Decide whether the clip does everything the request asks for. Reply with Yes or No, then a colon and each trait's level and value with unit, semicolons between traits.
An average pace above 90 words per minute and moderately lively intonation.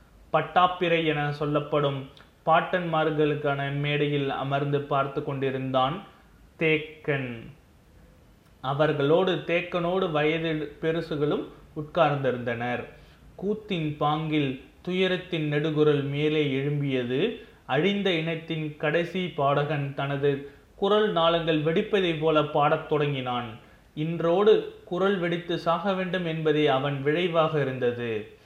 No: average, 85 wpm; average, 3.0 semitones